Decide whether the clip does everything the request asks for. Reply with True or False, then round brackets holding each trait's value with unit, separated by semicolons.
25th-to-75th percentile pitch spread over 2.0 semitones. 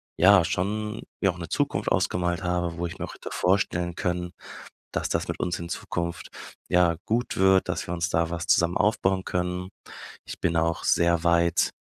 False (1.5 semitones)